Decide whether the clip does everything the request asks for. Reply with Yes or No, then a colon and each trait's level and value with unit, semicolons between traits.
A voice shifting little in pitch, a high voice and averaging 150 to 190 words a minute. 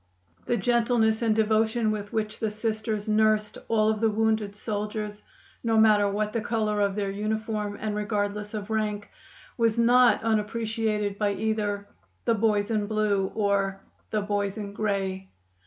Yes: narrow, 1.2 semitones; high, 215 Hz; average, 155 wpm